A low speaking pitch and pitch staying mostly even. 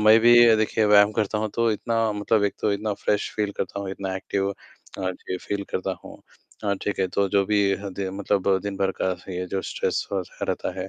Yes: low, 100 Hz; narrow, 1.7 semitones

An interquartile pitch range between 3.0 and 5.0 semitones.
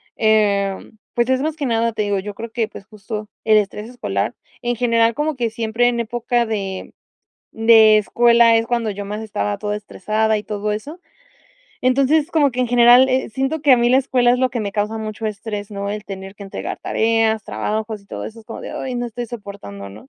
No: narrow, 2.6 semitones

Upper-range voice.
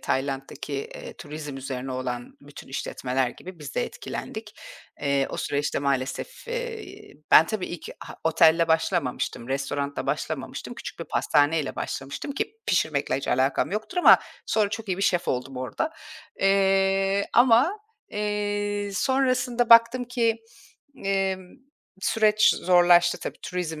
No: medium, 180 Hz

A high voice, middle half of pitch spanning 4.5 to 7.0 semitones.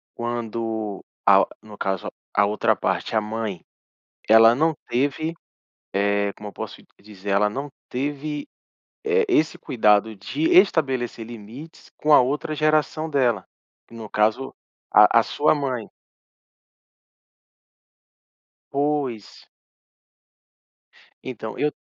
No: low, 120 Hz; wide, 5.5 semitones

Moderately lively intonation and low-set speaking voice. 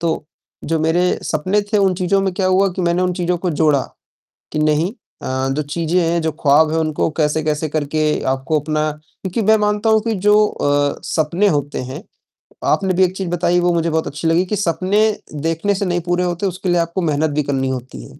No: average, 3.3 semitones; medium, 165 Hz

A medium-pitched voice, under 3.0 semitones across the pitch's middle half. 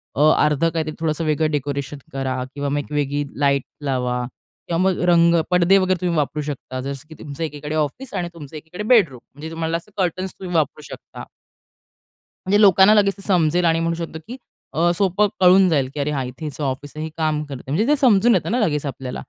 No: medium, 160 Hz; average, 3.8 semitones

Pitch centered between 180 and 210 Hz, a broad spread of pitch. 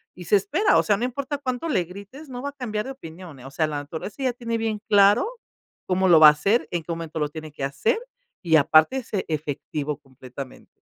Yes: medium, 185 Hz; wide, 8.1 semitones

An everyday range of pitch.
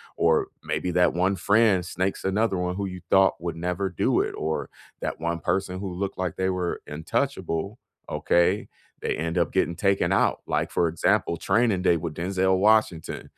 No: narrow, 2.3 semitones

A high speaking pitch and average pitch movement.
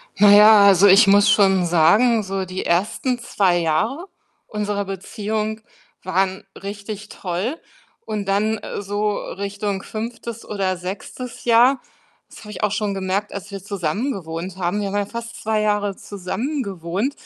No: high, 205 Hz; narrow, 2.2 semitones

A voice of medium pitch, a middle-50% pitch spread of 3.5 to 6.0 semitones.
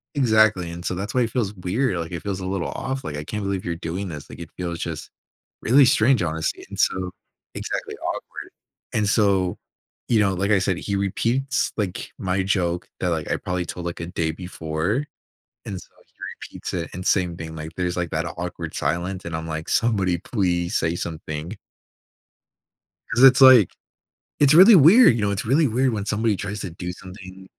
No: very low, 95 Hz; average, 3.9 semitones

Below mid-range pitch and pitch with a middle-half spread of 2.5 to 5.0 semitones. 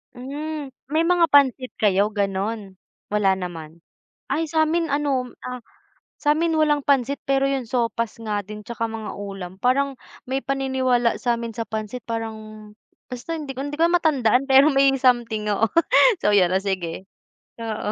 No: high, 245 Hz; average, 4.7 semitones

